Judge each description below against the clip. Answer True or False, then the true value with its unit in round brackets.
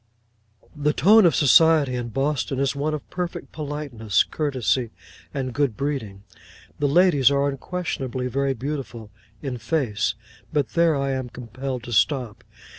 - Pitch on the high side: False (135 Hz)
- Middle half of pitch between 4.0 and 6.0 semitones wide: False (3.5 semitones)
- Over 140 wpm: False (135 wpm)